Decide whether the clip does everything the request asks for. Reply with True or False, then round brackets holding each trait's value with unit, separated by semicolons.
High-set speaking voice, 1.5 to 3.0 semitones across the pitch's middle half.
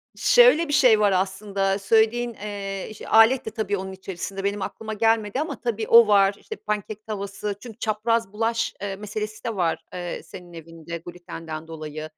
True (205 Hz; 2.7 semitones)